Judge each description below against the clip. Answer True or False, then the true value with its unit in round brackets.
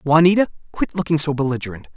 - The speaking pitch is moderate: True (150 Hz)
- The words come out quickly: False (155 wpm)